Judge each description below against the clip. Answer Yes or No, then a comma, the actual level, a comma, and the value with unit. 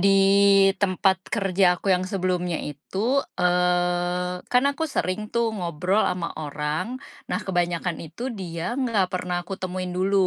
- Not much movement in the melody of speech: Yes, narrow, 1.4 semitones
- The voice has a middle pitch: Yes, medium, 180 Hz